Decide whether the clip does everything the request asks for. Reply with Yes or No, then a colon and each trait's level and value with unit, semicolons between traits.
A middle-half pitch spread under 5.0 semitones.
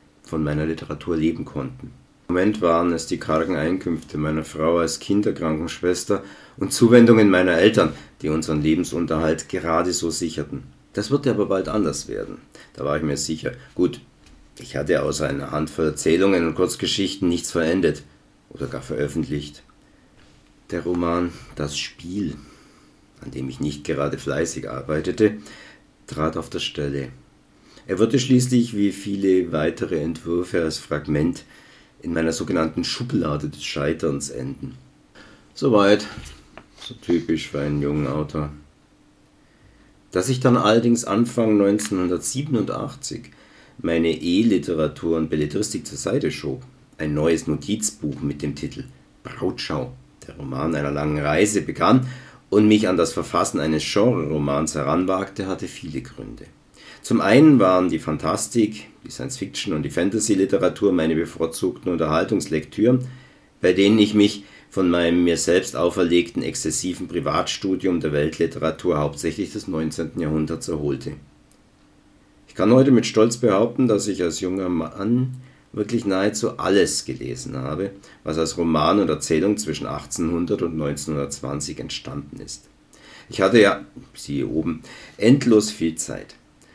No: average, 5.3 semitones